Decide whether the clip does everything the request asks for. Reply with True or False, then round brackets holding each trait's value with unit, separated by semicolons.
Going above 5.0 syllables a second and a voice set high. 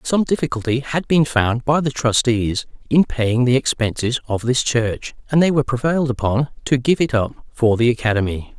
False (5.2 syllables/s; 125 Hz)